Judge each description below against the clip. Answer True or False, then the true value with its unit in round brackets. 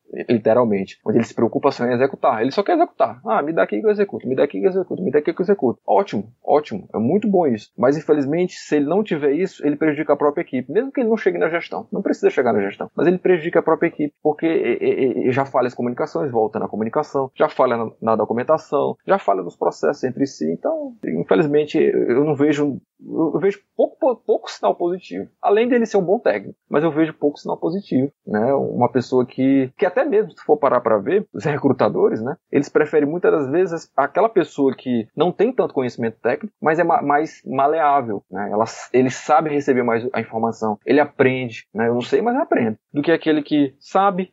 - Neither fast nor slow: False (220 wpm)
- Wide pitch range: True (7.4 semitones)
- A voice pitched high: False (150 Hz)